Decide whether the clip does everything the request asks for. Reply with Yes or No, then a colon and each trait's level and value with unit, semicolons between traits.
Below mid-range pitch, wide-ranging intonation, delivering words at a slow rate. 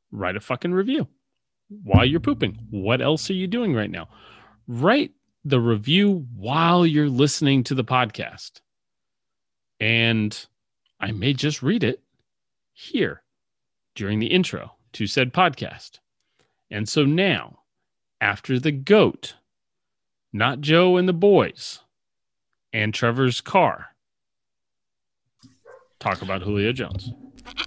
Yes: low, 130 Hz; wide, 7.9 semitones; slow, 115 wpm